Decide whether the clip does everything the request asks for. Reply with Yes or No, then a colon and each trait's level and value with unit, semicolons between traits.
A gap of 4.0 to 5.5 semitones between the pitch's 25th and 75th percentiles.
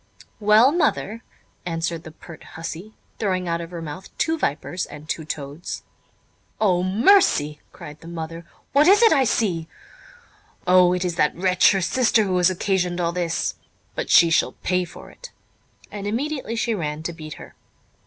Yes: average, 4.6 semitones